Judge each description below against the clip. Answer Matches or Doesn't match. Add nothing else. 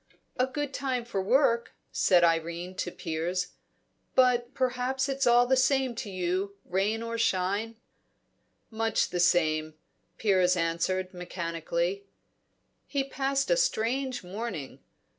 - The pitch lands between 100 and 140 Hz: Doesn't match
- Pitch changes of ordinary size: Doesn't match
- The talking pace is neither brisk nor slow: Doesn't match